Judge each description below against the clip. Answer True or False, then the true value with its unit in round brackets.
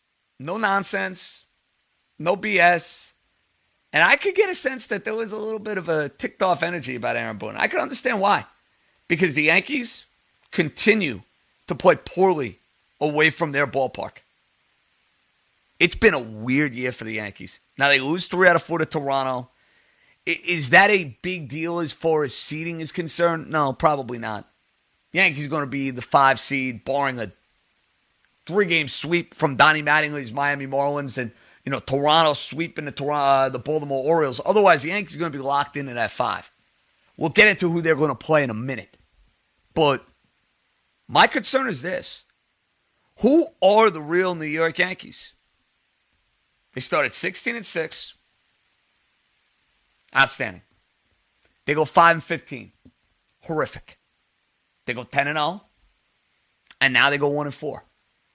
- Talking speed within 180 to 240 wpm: False (160 wpm)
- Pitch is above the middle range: False (155 Hz)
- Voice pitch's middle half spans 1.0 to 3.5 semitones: False (4.6 semitones)